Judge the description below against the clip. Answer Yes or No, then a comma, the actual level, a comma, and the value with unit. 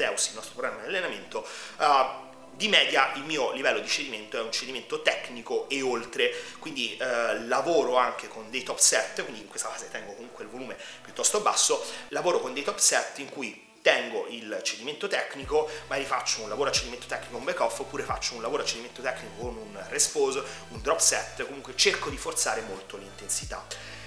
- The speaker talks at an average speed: No, fast, 190 wpm